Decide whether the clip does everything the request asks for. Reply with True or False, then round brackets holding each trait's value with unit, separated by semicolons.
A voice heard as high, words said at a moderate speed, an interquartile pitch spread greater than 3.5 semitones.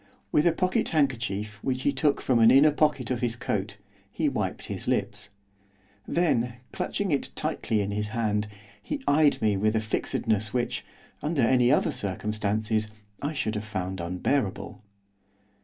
False (115 Hz; 155 wpm; 5.0 semitones)